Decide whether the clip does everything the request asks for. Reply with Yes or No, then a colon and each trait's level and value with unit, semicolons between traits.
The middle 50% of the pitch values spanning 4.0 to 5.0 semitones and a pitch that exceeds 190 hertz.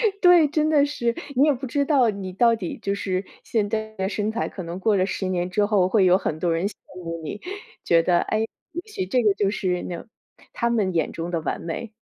Yes: average, 4.5 semitones; high, 205 Hz